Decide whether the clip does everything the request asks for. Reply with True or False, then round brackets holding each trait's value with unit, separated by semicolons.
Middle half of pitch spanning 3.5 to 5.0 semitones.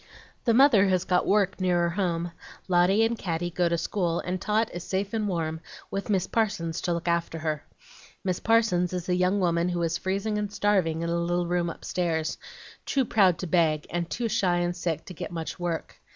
False (2.6 semitones)